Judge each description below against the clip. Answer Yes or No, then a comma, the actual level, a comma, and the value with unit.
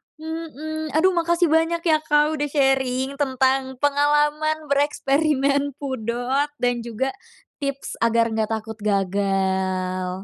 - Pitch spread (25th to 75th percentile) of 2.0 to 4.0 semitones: No, average, 4.6 semitones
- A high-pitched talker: Yes, very high, 275 Hz